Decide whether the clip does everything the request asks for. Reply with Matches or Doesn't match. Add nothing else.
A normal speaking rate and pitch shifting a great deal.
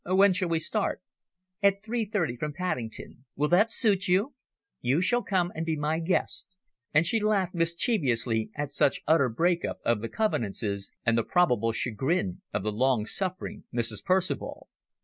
Matches